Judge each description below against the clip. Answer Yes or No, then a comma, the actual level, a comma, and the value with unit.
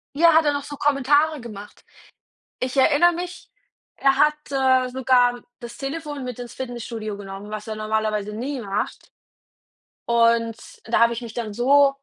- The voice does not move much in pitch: No, average, 4.1 semitones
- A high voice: Yes, very high, 250 Hz